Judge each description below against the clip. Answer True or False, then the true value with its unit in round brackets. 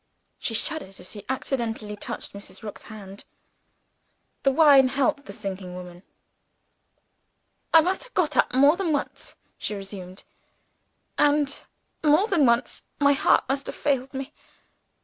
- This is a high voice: True (265 Hz)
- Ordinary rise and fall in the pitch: False (6.3 semitones)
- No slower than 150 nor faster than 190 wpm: False (140 wpm)